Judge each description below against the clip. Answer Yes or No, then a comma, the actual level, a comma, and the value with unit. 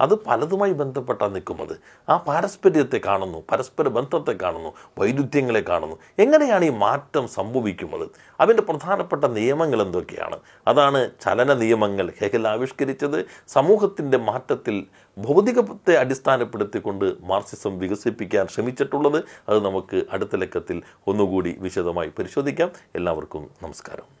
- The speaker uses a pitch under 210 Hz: Yes, medium, 140 Hz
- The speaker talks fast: No, average, 100 wpm